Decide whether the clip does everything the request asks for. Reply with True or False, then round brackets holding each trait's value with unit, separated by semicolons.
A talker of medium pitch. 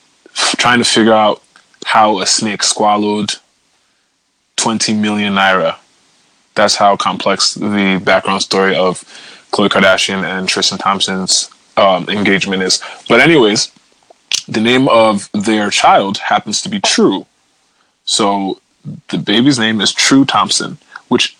False (105 Hz)